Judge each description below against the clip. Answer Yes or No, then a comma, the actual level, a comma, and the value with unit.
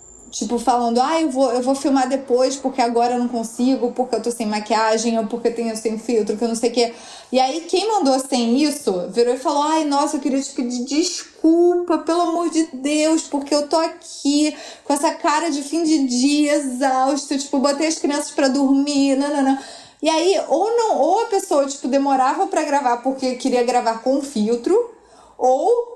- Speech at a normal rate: No, fast, 210 wpm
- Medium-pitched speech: No, very high, 275 Hz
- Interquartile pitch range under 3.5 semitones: No, average, 4.4 semitones